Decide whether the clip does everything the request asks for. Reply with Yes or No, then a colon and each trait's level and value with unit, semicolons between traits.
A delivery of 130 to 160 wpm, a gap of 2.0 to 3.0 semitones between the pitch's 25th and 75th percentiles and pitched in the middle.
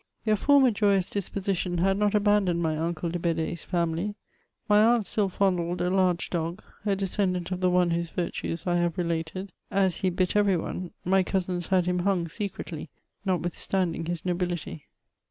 No: average, 170 wpm; narrow, 2.4 semitones; medium, 180 Hz